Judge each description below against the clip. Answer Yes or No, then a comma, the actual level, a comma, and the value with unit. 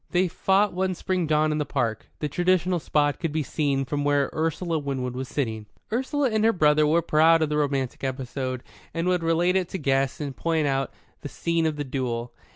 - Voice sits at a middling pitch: Yes, medium, 150 Hz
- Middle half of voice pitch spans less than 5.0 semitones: Yes, average, 4.1 semitones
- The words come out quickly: Yes, fast, 210 wpm